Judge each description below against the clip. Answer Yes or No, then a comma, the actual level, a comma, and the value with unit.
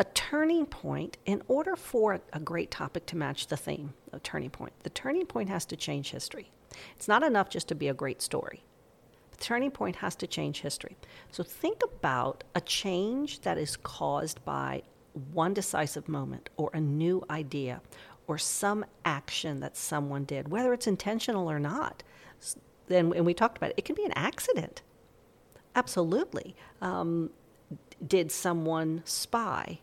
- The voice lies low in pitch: No, medium, 180 Hz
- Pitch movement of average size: No, wide, 7.5 semitones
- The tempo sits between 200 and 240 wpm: No, average, 165 wpm